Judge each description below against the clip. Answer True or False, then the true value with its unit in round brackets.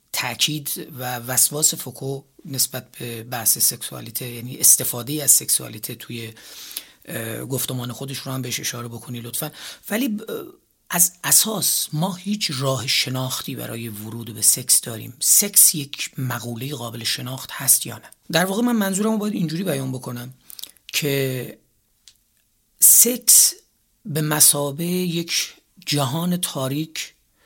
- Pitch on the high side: False (135 Hz)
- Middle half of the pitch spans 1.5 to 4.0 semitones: False (5.2 semitones)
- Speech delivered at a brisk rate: False (125 wpm)